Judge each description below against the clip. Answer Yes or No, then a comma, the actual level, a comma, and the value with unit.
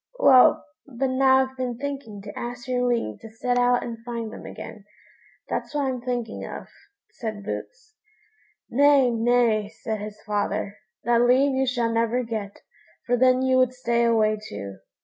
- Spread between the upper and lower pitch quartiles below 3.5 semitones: Yes, narrow, 2.6 semitones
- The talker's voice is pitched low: No, high, 240 Hz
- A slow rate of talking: No, average, 170 wpm